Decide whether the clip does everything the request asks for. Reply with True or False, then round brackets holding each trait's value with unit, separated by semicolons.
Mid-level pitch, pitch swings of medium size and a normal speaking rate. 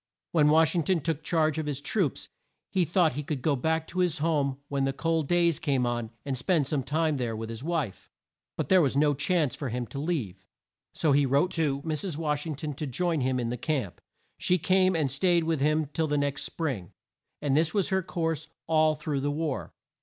False (150 Hz; 3.0 semitones; 225 wpm)